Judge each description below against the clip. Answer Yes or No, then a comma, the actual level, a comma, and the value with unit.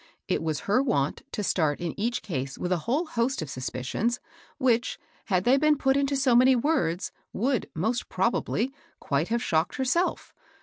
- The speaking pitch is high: Yes, high, 230 Hz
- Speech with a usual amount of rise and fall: No, wide, 8.0 semitones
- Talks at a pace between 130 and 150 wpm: No, average, 175 wpm